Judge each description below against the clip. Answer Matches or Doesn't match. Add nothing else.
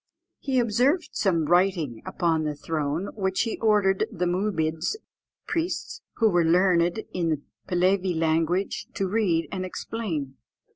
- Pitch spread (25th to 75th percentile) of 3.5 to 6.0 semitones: Matches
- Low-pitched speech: Doesn't match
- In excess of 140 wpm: Doesn't match